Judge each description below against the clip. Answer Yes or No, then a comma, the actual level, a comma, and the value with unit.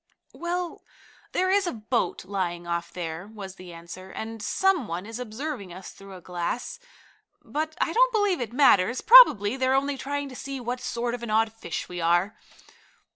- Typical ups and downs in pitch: No, wide, 7.4 semitones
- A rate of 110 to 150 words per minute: No, average, 180 wpm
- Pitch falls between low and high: No, high, 225 Hz